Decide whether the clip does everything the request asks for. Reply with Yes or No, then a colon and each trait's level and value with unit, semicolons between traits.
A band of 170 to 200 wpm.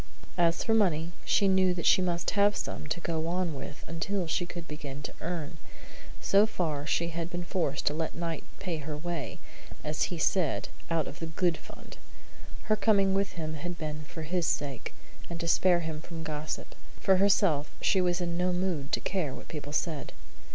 Yes: average, 195 wpm